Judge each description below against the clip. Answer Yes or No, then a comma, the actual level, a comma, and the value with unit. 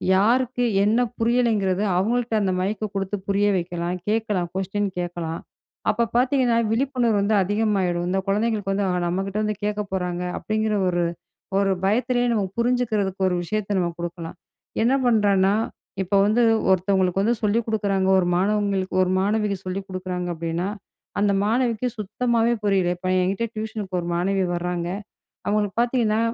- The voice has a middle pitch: No, high, 200 Hz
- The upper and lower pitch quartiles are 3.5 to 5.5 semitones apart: No, average, 3.1 semitones